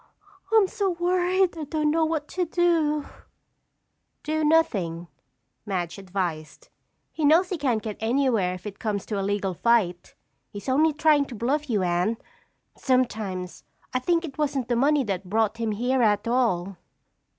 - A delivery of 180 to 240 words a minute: No, average, 160 wpm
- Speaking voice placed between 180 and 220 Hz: No, high, 245 Hz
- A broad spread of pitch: Yes, wide, 7.4 semitones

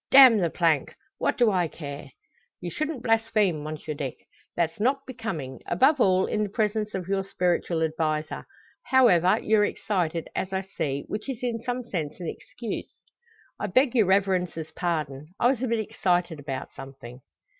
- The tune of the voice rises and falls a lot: Yes, wide, 6.0 semitones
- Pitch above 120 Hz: Yes, medium, 185 Hz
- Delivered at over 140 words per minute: Yes, average, 165 wpm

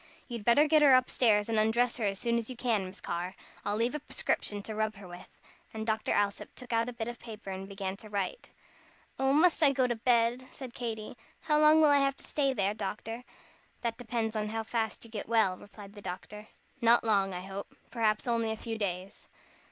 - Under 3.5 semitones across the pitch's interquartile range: Yes, average, 3.1 semitones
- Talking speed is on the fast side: Yes, fast, 225 wpm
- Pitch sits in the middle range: No, high, 225 Hz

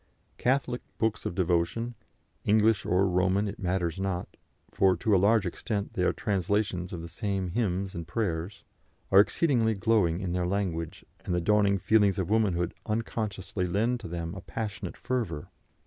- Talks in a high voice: No, very low, 95 Hz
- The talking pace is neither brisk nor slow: Yes, average, 165 wpm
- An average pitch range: Yes, average, 3.4 semitones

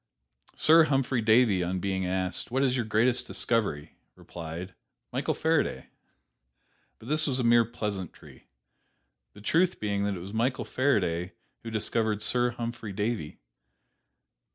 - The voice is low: Yes, low, 110 Hz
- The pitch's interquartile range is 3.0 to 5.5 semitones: Yes, average, 4.4 semitones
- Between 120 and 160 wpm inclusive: Yes, slow, 135 wpm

